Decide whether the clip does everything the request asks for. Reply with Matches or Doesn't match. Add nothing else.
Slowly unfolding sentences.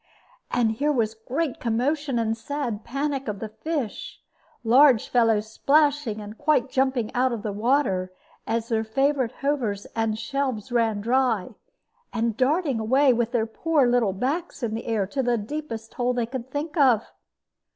Doesn't match